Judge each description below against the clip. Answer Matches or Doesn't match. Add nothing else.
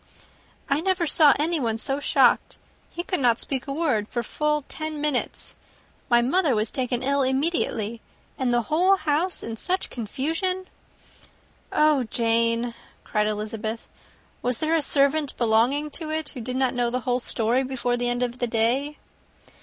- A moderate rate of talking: Matches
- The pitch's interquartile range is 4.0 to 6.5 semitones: Matches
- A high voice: Matches